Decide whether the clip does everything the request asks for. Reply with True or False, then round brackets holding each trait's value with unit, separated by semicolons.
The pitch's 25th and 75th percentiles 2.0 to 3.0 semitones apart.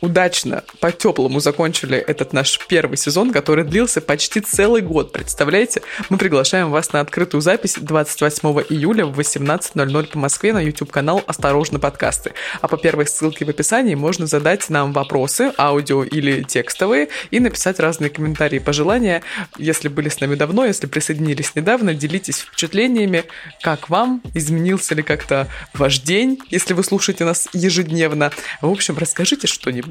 False (4.1 semitones)